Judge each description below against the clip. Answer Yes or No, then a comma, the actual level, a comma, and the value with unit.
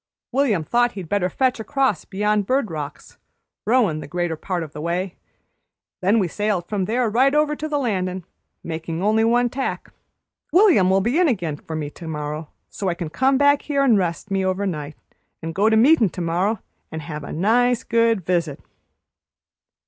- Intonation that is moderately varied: No, wide, 6.3 semitones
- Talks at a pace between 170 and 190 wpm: Yes, average, 185 wpm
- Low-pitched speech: No, high, 195 Hz